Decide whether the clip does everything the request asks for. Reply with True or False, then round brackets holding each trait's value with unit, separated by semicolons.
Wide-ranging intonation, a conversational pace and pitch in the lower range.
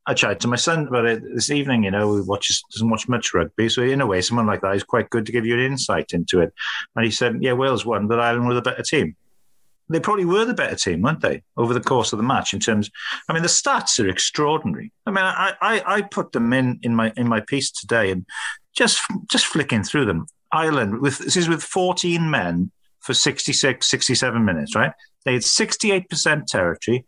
False (6.1 semitones; 230 wpm; 125 Hz)